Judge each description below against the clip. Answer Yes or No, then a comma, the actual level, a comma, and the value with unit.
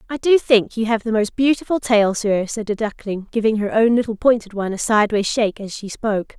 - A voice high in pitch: Yes, high, 220 Hz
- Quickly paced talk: Yes, fast, 235 wpm